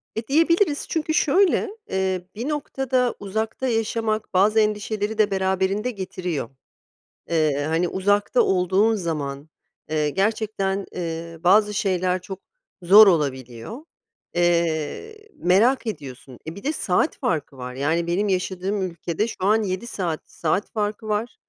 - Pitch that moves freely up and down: No, average, 4.4 semitones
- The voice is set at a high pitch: Yes, high, 195 Hz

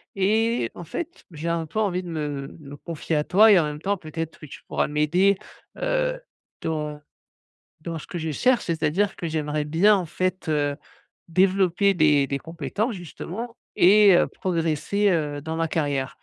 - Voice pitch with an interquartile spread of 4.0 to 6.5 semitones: Yes, average, 4.6 semitones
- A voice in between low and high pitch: Yes, medium, 165 Hz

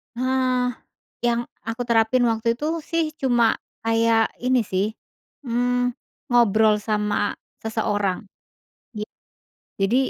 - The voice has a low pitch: No, high, 230 Hz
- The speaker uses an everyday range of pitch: No, narrow, 2.2 semitones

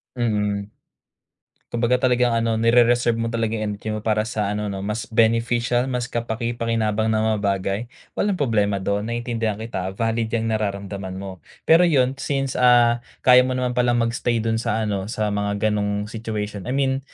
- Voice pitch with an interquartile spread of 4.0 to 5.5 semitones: No, narrow, 2.6 semitones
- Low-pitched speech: Yes, low, 115 Hz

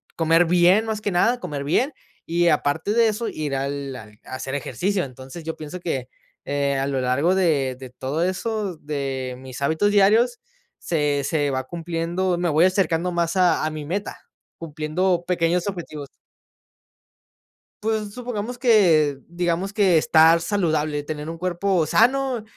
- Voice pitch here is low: No, medium, 165 Hz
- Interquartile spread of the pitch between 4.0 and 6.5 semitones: Yes, average, 4.7 semitones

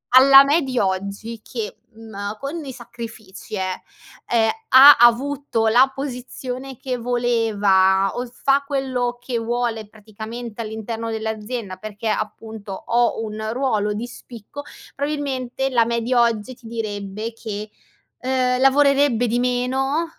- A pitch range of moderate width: Yes, average, 3.0 semitones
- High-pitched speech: Yes, high, 235 Hz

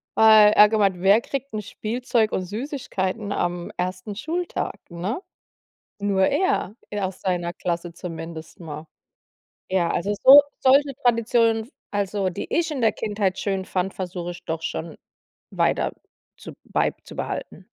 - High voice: Yes, high, 200 Hz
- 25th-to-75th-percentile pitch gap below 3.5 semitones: No, average, 4.1 semitones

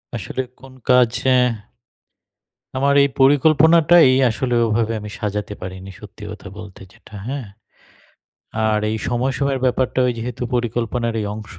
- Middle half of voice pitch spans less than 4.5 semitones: Yes, average, 3.8 semitones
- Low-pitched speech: Yes, low, 120 Hz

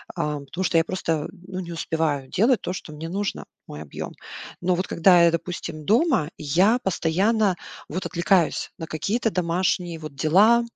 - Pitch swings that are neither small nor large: Yes, average, 3.2 semitones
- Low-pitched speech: No, medium, 175 Hz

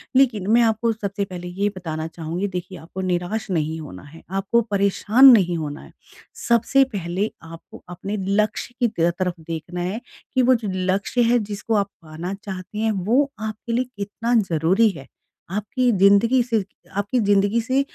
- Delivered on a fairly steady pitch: No, average, 4.1 semitones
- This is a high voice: Yes, high, 200 Hz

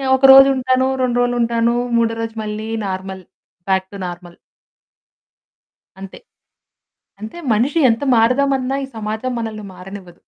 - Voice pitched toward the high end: Yes, high, 225 Hz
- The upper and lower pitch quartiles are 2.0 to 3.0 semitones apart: No, average, 4.3 semitones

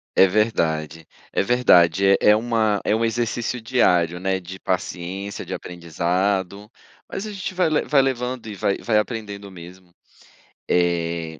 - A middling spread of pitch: Yes, average, 4.6 semitones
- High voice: No, low, 100 Hz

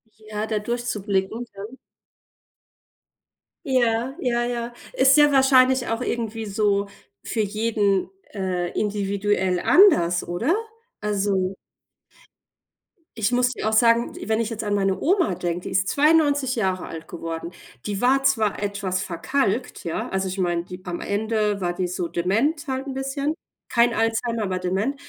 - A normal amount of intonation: Yes, average, 4.4 semitones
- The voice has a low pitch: No, high, 215 Hz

